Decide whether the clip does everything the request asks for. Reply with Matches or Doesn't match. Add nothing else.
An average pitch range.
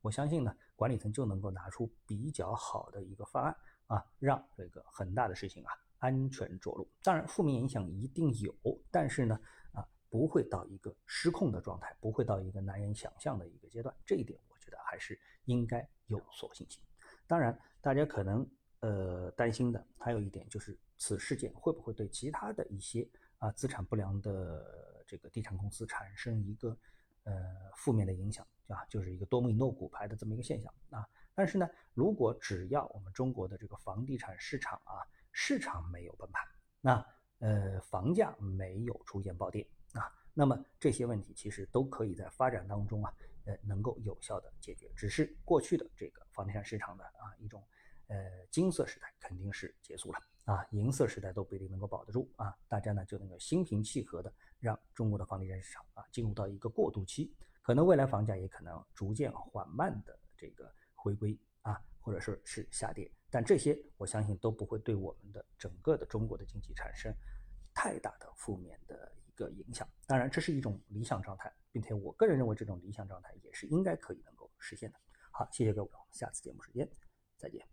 Matches